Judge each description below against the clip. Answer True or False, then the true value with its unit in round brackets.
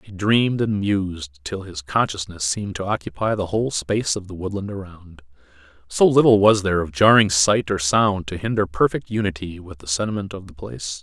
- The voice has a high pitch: False (95 Hz)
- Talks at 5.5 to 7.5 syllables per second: True (5.6 syllables/s)